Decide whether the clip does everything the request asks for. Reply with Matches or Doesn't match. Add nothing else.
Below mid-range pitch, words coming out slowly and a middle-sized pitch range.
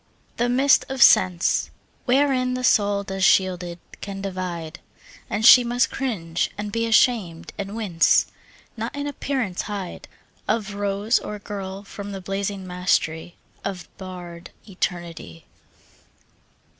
Doesn't match